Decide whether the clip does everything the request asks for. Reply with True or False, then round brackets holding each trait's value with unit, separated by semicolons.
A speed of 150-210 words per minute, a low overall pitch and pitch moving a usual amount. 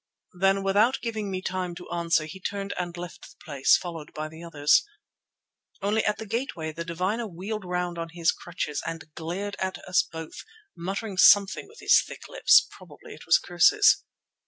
False (180 wpm; 180 Hz; 3.3 semitones)